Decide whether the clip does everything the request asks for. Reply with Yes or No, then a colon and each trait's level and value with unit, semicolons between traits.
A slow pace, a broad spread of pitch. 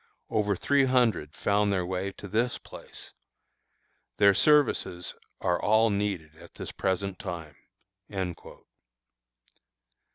No: slow, 105 wpm; average, 3.3 semitones